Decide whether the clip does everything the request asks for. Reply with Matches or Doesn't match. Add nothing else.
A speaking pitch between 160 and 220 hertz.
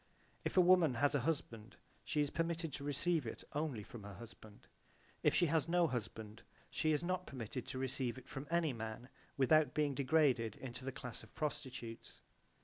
Doesn't match